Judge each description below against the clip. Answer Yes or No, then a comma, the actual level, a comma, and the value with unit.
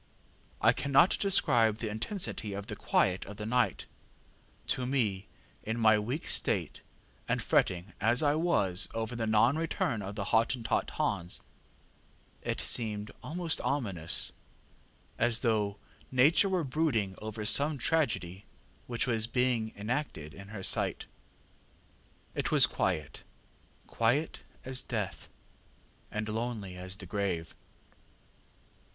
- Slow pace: Yes, slow, 125 wpm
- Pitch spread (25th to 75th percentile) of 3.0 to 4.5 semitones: Yes, average, 4.2 semitones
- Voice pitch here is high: No, low, 110 Hz